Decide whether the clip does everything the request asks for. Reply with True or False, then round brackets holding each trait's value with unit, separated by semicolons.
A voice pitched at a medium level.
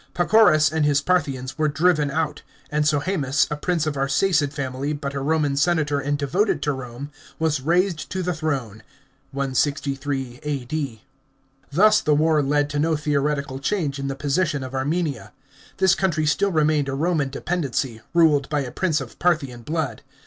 True (150 Hz)